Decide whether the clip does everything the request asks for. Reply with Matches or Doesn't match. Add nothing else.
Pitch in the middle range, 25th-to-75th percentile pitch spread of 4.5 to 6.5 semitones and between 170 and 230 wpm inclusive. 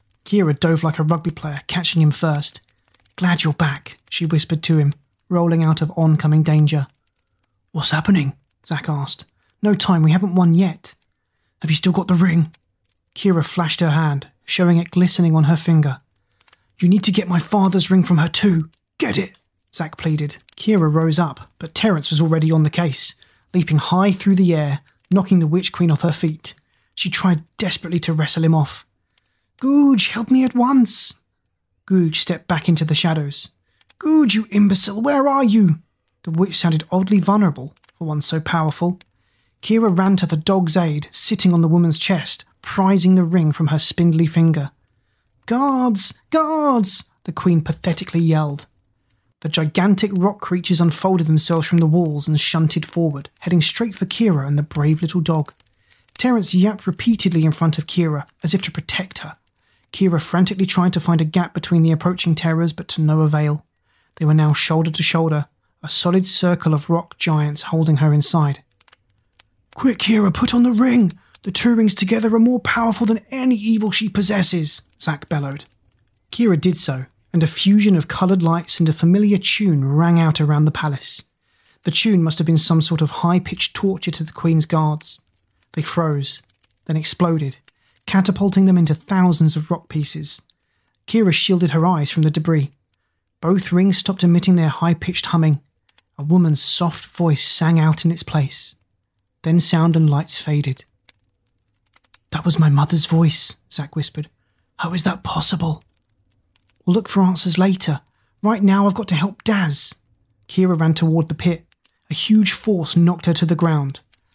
Doesn't match